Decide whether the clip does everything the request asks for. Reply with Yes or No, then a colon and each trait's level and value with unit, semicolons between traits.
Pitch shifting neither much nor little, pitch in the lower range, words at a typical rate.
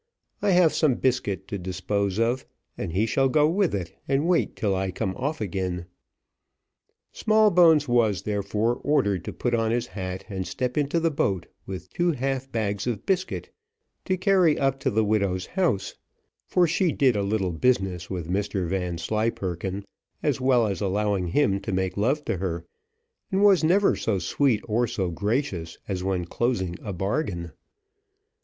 No: wide, 6.4 semitones; low, 110 Hz; average, 165 wpm